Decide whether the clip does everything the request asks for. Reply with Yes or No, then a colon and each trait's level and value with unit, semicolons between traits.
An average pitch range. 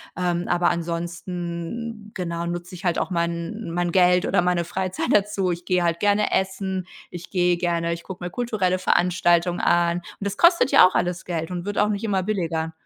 No: narrow, 1.8 semitones